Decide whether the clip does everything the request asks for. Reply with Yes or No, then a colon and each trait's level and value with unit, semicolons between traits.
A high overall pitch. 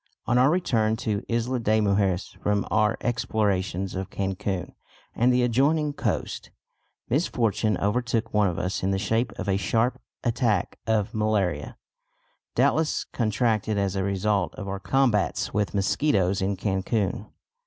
No: low, 105 Hz